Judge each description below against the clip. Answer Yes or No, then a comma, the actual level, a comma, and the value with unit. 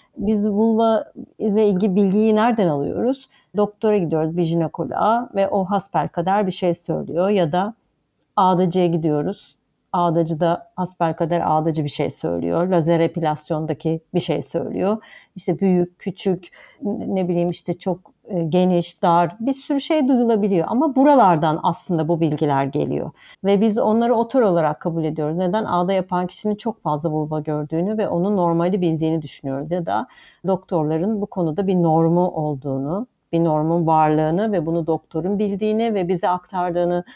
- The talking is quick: Yes, fast, 150 wpm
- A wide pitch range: No, average, 3.9 semitones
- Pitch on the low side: No, medium, 180 Hz